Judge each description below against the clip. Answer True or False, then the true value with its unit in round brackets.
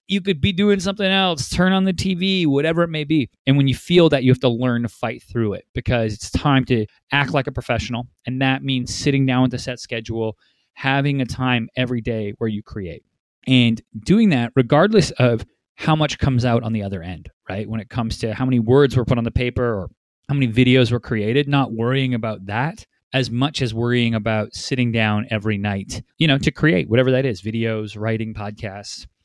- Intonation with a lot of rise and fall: False (3.8 semitones)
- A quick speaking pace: True (220 wpm)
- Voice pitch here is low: True (125 Hz)